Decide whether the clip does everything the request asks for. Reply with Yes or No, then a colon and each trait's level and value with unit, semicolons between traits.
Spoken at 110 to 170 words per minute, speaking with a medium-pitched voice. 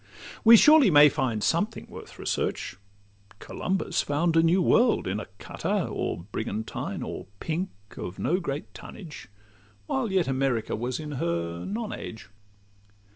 Yes: average, 140 wpm; medium, 150 Hz